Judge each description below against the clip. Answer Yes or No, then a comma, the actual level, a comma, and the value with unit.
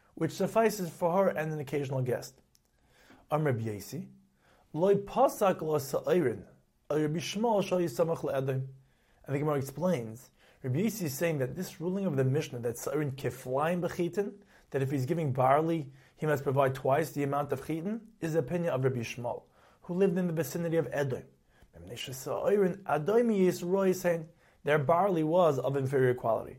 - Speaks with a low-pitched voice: No, medium, 155 Hz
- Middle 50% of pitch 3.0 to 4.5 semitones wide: No, average, 5.0 semitones